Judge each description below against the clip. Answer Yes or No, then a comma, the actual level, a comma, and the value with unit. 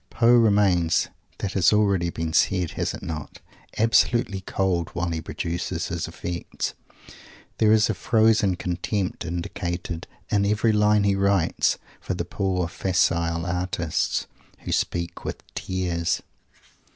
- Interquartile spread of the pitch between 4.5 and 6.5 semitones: No, average, 3.2 semitones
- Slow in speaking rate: Yes, slow, 130 wpm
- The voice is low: Yes, very low, 90 Hz